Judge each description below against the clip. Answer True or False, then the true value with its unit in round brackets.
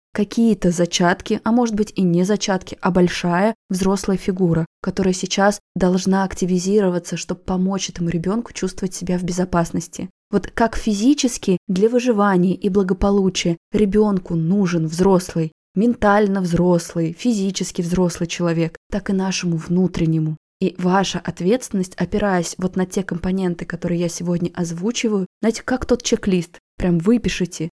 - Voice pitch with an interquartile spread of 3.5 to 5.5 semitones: False (2.6 semitones)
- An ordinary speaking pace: True (130 wpm)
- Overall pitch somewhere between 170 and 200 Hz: True (185 Hz)